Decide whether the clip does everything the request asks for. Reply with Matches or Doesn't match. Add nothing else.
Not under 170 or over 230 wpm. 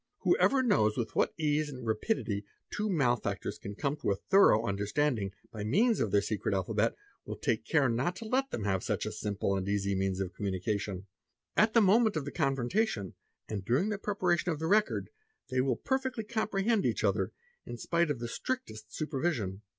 Matches